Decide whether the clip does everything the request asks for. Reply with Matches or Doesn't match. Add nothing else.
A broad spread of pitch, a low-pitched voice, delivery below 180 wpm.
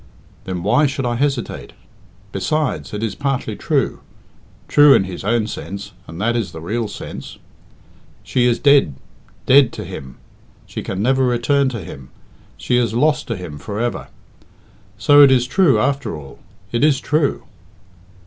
Matches